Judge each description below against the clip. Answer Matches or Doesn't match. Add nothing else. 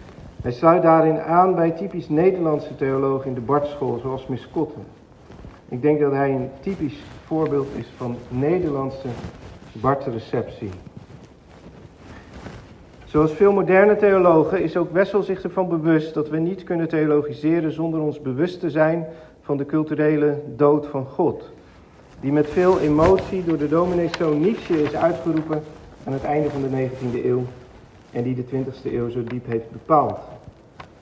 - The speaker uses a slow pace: Doesn't match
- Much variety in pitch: Doesn't match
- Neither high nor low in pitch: Matches